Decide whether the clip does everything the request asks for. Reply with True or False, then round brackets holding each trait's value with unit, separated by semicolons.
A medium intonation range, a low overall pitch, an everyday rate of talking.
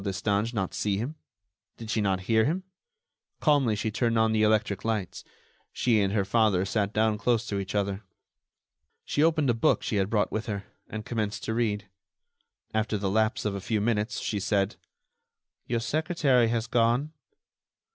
False (2.3 semitones; 110 Hz; 175 wpm)